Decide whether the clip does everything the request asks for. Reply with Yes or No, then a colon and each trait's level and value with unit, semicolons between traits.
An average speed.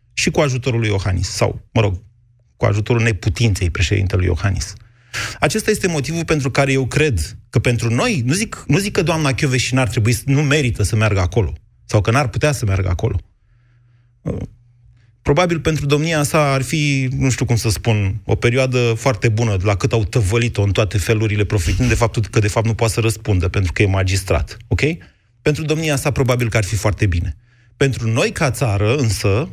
No: fast, 195 wpm